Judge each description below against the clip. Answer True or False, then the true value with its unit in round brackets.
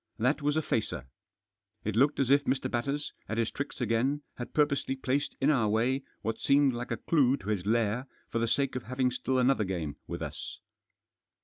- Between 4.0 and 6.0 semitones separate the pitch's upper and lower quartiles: False (3.6 semitones)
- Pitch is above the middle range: False (130 Hz)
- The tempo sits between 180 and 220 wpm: True (200 wpm)